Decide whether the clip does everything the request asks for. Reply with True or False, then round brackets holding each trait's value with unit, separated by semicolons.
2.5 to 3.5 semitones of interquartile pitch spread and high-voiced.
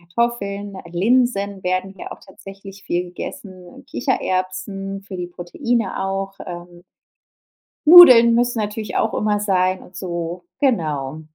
True (2.9 semitones; 195 Hz)